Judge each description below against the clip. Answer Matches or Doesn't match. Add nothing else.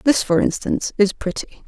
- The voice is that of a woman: Matches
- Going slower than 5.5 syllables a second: Matches